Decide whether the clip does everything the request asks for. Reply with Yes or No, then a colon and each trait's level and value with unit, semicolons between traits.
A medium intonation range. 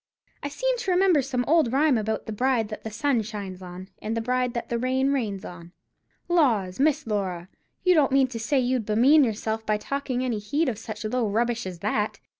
Yes: average, 4.5 semitones